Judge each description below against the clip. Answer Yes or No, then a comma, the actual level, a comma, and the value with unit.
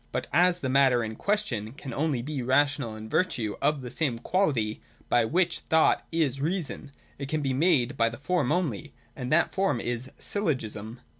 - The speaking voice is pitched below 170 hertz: Yes, medium, 140 Hz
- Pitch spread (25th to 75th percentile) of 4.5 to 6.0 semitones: Yes, average, 5.2 semitones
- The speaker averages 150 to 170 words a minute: No, average, 190 wpm